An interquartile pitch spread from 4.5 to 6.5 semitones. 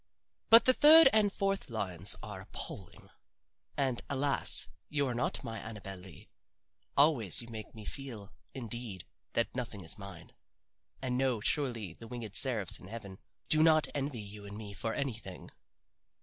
Yes: average, 5.3 semitones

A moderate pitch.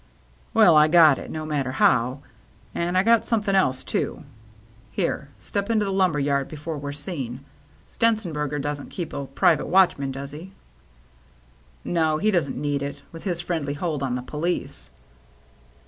Yes: medium, 150 Hz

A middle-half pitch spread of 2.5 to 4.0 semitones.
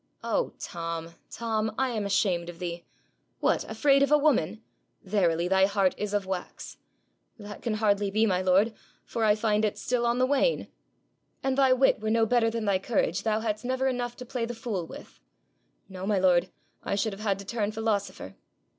Yes: average, 3.7 semitones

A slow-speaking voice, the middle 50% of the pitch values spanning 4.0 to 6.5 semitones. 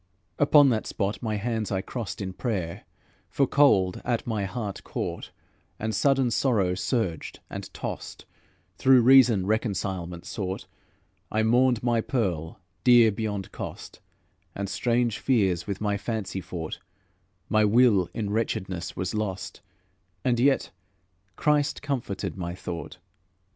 Yes: slow, 130 wpm; average, 4.3 semitones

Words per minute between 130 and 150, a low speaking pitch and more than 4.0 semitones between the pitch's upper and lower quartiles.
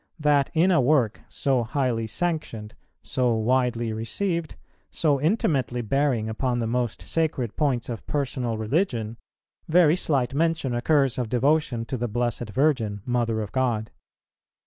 Yes: average, 140 wpm; low, 125 Hz; average, 4.4 semitones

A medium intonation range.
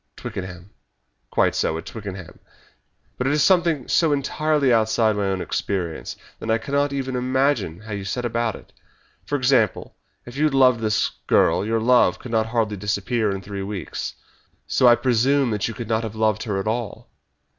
Yes: average, 4.0 semitones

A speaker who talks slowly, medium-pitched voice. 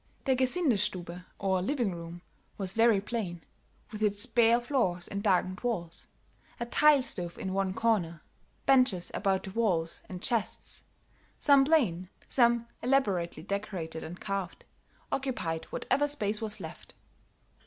No: slow, 130 wpm; high, 200 Hz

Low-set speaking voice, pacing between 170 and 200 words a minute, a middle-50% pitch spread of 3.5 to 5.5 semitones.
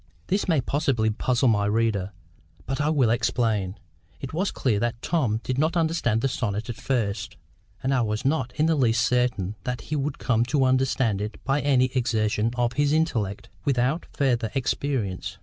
Yes: low, 125 Hz; average, 180 wpm; average, 3.9 semitones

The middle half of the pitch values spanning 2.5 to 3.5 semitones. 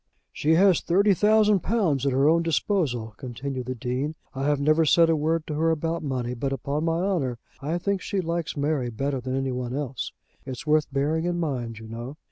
No: average, 4.2 semitones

